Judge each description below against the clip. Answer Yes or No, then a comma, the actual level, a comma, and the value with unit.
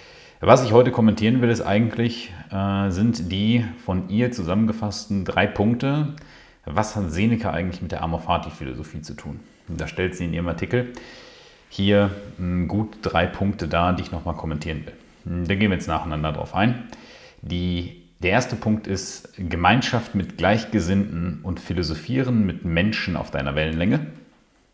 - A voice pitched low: Yes, very low, 95 Hz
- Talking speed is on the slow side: No, average, 155 wpm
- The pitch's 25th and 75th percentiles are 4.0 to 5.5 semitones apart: Yes, average, 4.5 semitones